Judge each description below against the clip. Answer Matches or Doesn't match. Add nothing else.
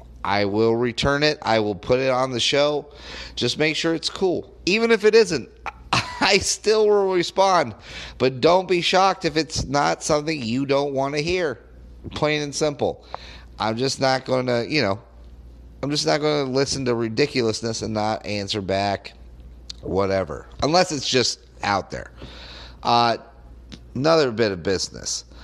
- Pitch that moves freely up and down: Matches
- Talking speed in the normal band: Matches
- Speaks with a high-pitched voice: Doesn't match